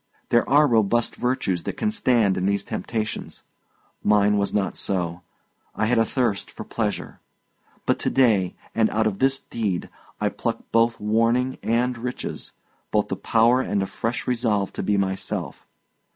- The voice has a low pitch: Yes, low, 110 Hz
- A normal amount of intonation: Yes, average, 3.5 semitones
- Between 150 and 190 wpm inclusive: Yes, average, 165 wpm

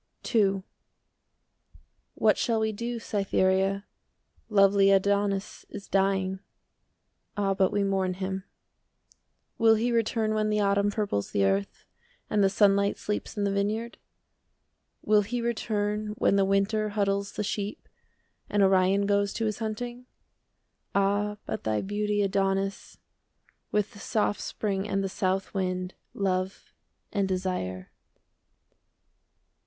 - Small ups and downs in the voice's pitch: Yes, narrow, 1.5 semitones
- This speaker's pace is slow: Yes, slow, 130 wpm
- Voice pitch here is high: Yes, high, 200 Hz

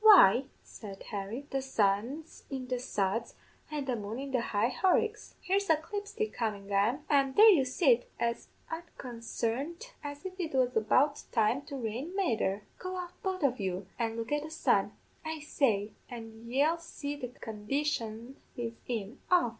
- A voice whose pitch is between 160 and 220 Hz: No, very high, 260 Hz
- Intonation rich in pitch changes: Yes, wide, 5.8 semitones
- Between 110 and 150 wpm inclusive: No, average, 165 wpm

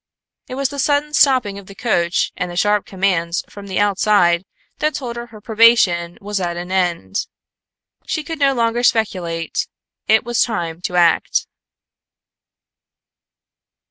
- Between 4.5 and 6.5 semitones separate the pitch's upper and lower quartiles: Yes, average, 5.3 semitones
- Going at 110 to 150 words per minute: Yes, average, 145 wpm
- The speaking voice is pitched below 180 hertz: No, high, 205 Hz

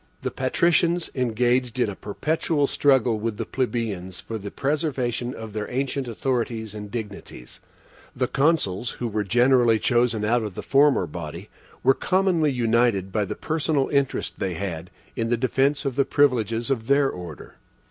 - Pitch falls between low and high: No, low, 120 Hz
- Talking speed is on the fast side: No, average, 160 wpm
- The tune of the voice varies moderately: Yes, average, 4.2 semitones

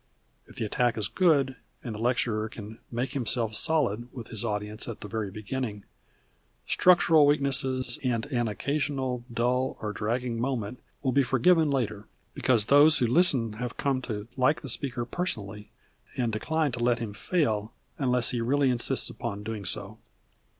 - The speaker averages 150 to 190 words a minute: Yes, average, 165 wpm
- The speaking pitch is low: Yes, low, 120 Hz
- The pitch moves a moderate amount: Yes, average, 3.7 semitones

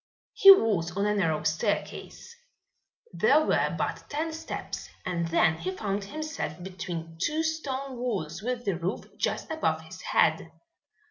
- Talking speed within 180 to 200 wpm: No, average, 145 wpm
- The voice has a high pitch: Yes, high, 205 Hz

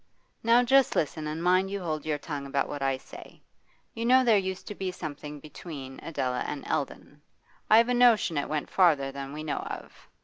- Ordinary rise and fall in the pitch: No, wide, 5.9 semitones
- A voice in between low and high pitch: Yes, medium, 155 Hz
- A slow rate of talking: No, average, 200 wpm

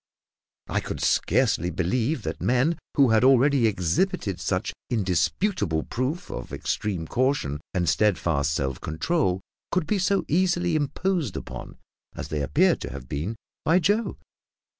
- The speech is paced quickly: No, average, 140 wpm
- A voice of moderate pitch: No, low, 120 Hz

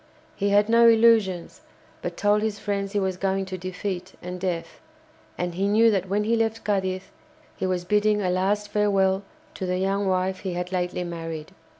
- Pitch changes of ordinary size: No, narrow, 2.2 semitones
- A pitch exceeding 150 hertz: Yes, high, 190 Hz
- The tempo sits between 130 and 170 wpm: No, average, 190 wpm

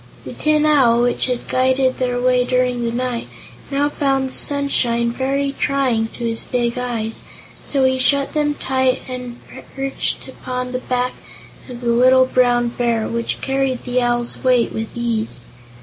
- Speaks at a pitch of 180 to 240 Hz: No, very high, 250 Hz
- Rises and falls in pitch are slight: Yes, narrow, 1.8 semitones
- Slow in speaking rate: No, average, 165 wpm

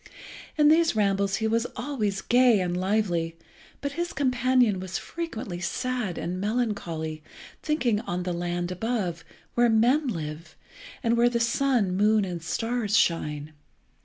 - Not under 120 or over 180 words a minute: Yes, average, 140 wpm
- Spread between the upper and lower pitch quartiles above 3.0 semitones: Yes, wide, 5.5 semitones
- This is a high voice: Yes, high, 215 Hz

